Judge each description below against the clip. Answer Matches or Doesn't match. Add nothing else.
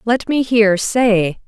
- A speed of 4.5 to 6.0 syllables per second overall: Doesn't match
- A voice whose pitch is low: Doesn't match